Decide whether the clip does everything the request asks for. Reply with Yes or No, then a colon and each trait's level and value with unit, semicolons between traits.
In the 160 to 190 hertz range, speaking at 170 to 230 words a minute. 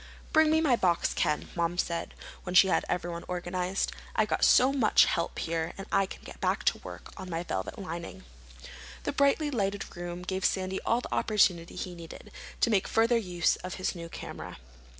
Yes: medium, 185 Hz; average, 190 wpm